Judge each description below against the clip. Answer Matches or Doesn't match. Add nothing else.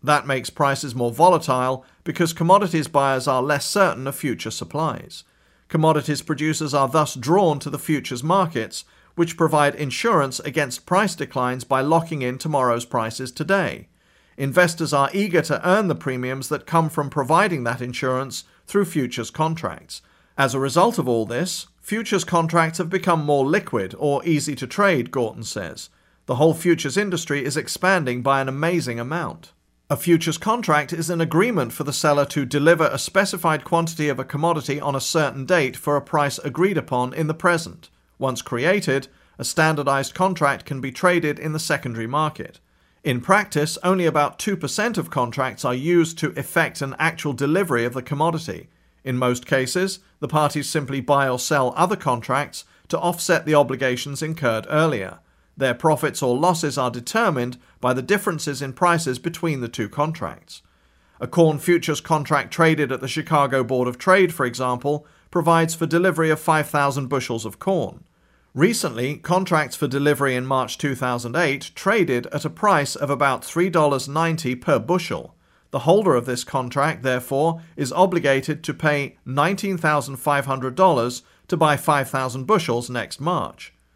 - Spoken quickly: Doesn't match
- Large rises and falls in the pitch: Doesn't match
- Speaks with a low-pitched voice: Doesn't match